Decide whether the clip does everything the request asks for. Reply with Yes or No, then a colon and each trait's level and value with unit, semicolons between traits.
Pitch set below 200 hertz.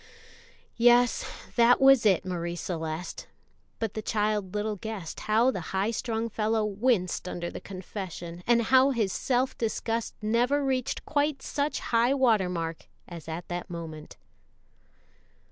No: high, 215 Hz